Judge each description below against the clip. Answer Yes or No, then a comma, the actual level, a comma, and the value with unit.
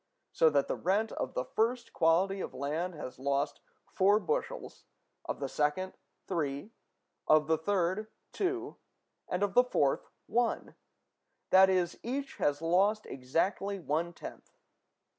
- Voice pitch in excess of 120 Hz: Yes, medium, 185 Hz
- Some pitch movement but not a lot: No, wide, 5.7 semitones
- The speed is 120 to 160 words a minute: Yes, average, 140 wpm